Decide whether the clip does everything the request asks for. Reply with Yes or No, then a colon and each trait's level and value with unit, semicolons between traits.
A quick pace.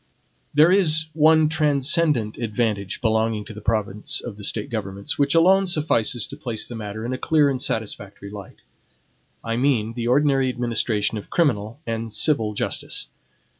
No: average, 160 wpm